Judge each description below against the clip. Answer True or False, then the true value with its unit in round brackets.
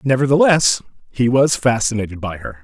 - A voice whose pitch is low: True (125 Hz)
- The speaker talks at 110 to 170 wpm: True (135 wpm)